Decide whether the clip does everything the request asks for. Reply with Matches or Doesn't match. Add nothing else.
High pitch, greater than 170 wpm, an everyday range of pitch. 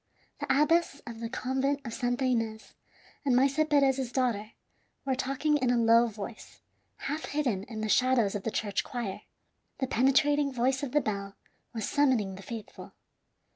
Doesn't match